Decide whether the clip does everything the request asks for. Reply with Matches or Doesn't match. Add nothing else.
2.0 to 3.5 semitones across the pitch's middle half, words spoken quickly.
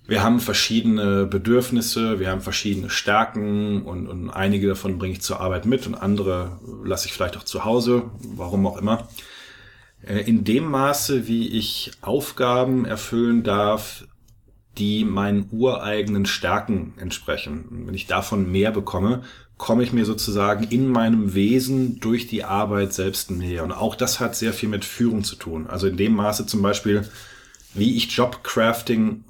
Doesn't match